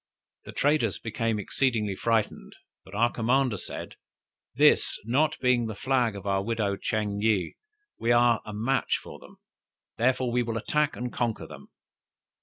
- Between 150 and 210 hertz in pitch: No, low, 115 Hz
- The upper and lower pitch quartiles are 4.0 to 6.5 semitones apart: No, average, 2.9 semitones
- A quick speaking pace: No, average, 155 wpm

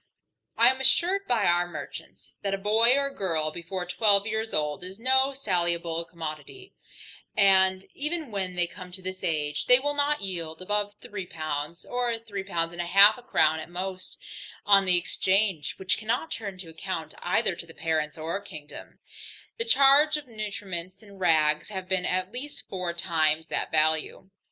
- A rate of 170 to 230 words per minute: Yes, average, 175 wpm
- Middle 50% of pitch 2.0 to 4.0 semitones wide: No, average, 4.6 semitones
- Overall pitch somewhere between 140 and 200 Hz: Yes, high, 190 Hz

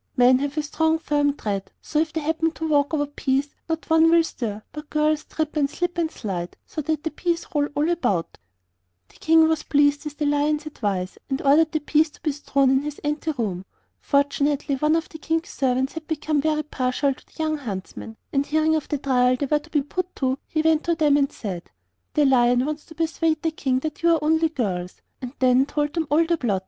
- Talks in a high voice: Yes, very high, 295 Hz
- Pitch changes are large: No, average, 2.9 semitones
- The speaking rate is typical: No, fast, 230 wpm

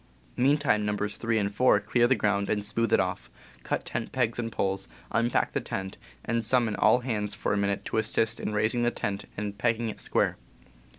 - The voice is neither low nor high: No, low, 110 Hz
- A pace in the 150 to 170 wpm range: No, average, 200 wpm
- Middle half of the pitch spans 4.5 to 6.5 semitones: No, narrow, 2.5 semitones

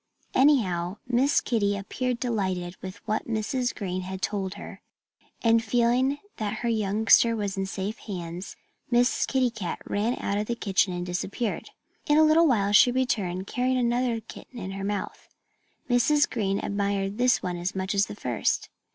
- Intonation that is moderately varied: Yes, average, 4.1 semitones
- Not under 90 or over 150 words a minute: No, average, 165 wpm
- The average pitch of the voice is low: No, high, 210 Hz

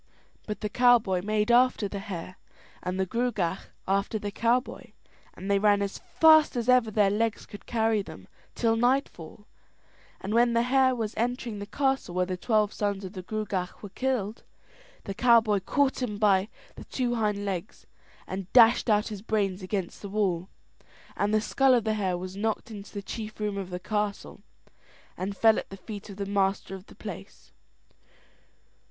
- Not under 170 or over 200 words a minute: Yes, average, 180 wpm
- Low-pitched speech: No, high, 210 Hz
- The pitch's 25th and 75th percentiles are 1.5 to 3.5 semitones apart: Yes, average, 3.0 semitones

